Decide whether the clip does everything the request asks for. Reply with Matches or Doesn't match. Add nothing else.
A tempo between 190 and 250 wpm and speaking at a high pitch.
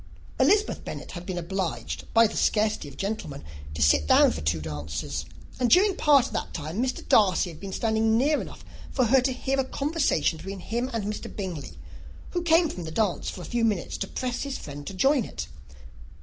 Matches